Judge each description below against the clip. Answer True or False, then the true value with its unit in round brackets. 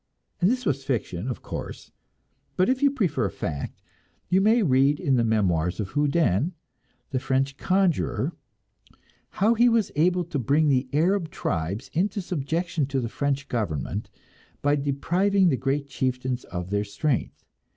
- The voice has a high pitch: False (140 Hz)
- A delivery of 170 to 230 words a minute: False (150 wpm)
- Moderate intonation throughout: False (6.3 semitones)